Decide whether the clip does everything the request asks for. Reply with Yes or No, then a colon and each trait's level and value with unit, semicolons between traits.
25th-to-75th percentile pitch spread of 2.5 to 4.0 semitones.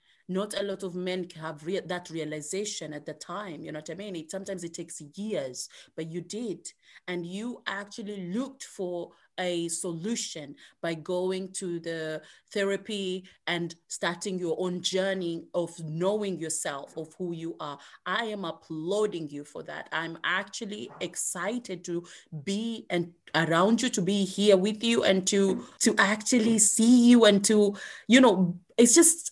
Yes: average, 3.6 semitones